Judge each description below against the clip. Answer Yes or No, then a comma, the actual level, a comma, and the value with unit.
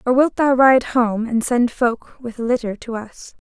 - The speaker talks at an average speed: No, fast, 225 wpm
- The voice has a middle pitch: No, high, 240 Hz